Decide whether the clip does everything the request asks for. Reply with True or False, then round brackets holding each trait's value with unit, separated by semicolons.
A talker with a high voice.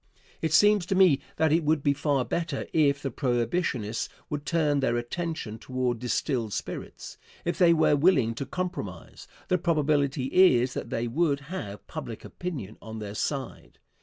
False (140 Hz)